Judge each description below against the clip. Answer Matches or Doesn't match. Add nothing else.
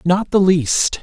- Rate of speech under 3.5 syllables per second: Matches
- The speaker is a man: Matches